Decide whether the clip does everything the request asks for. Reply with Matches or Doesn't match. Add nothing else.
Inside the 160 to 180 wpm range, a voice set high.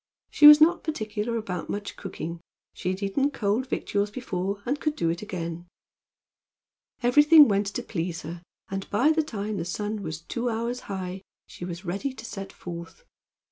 Matches